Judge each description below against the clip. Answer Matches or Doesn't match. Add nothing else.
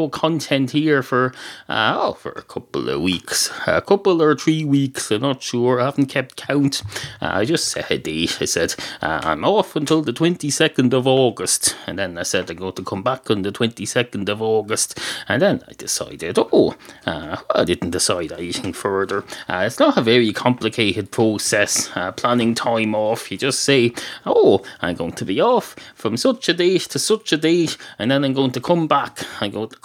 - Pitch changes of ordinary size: Doesn't match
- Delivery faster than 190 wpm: Matches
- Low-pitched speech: Matches